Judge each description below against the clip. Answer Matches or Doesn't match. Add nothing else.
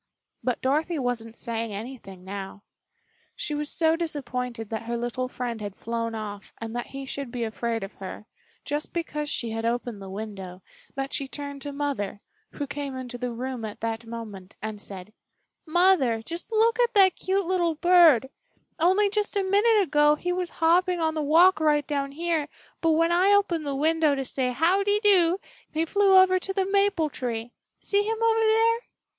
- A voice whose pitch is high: Matches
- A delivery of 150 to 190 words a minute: Matches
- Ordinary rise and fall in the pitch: Doesn't match